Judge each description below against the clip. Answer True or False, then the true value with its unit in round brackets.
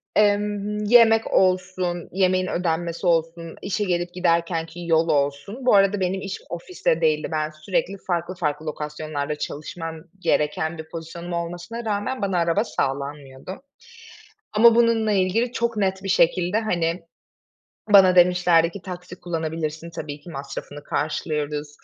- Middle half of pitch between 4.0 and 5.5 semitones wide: False (3.5 semitones)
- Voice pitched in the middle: True (175 Hz)